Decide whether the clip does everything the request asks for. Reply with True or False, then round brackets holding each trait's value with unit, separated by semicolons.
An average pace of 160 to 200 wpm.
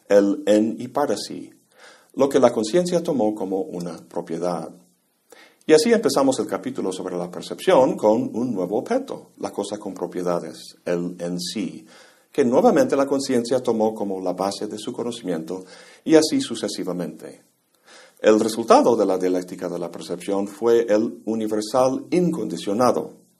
False (150 wpm)